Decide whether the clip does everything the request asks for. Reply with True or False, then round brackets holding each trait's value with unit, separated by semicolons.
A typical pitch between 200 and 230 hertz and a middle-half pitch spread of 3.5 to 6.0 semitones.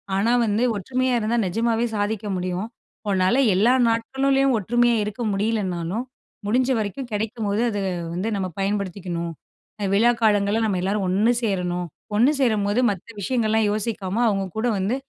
False (210 Hz; 3.1 semitones)